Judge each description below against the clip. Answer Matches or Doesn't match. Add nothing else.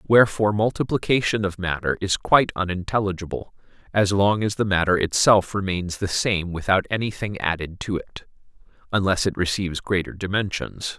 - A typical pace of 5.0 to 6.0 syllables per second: Matches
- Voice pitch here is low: Matches